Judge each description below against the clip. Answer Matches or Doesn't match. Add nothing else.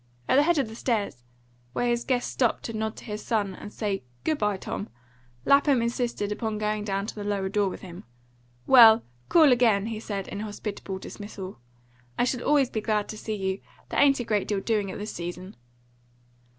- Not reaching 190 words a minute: Doesn't match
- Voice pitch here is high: Matches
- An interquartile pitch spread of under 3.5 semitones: Matches